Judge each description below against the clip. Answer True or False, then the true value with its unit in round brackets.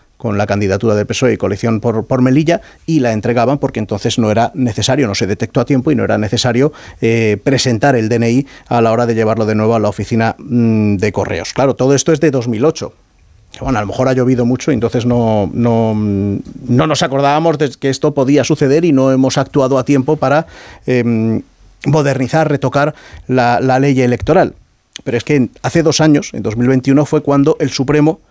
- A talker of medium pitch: False (125 Hz)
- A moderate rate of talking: False (200 wpm)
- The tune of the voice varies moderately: True (3.9 semitones)